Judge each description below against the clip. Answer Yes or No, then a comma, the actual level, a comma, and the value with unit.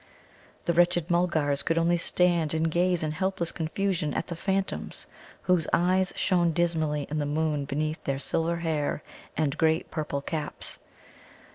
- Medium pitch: Yes, medium, 165 Hz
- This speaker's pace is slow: No, average, 150 wpm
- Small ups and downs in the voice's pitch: Yes, narrow, 2.3 semitones